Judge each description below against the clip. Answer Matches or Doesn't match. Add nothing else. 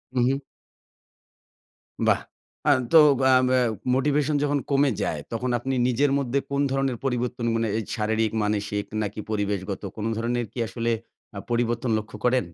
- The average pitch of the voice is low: Matches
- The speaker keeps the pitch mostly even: Doesn't match